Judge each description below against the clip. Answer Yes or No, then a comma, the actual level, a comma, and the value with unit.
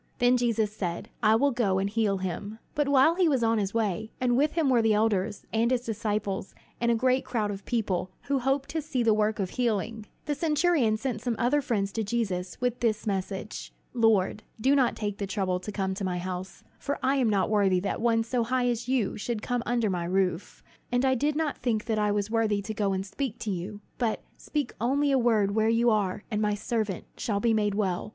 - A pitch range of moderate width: Yes, average, 3.4 semitones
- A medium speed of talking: No, fast, 230 wpm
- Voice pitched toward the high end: Yes, high, 220 Hz